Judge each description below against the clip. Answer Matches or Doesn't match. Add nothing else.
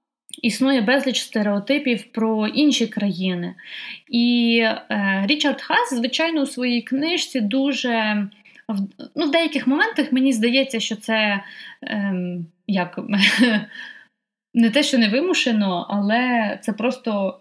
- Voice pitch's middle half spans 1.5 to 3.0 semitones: Doesn't match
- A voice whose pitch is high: Matches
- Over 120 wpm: Doesn't match